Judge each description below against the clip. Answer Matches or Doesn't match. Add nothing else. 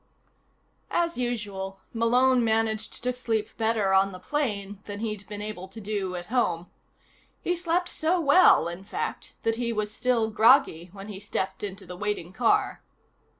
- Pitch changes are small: Doesn't match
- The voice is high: Matches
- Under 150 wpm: Doesn't match